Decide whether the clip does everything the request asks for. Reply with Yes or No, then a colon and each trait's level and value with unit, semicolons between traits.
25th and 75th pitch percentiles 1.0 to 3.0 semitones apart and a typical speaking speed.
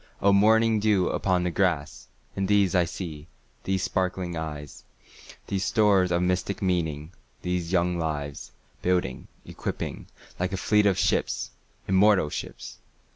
No: narrow, 2.6 semitones; slow, 110 wpm